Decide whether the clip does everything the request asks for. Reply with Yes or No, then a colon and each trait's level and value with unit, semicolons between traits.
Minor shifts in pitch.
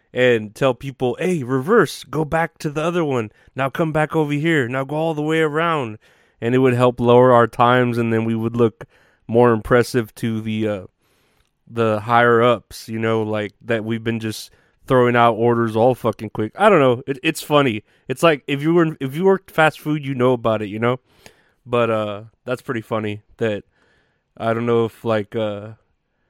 No: average, 3.7 semitones